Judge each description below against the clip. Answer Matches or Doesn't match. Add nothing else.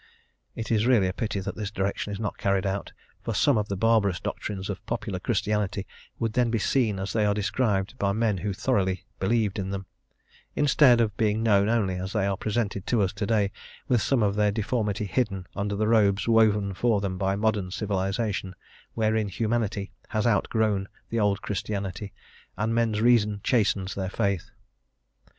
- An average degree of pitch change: Doesn't match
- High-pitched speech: Doesn't match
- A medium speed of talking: Matches